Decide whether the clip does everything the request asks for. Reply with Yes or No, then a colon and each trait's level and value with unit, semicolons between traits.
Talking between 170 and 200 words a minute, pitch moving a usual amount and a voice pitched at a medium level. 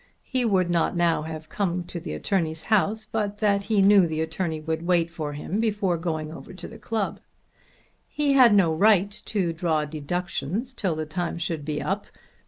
Yes: average, 190 wpm; average, 4.2 semitones; medium, 175 Hz